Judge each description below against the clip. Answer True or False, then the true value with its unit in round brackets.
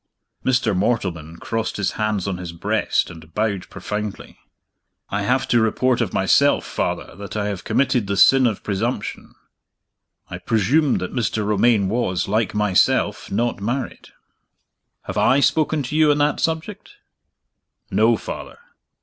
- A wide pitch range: False (4.4 semitones)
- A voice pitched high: False (110 Hz)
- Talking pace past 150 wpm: False (145 wpm)